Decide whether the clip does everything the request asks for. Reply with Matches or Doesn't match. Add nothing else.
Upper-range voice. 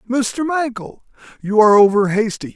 Matches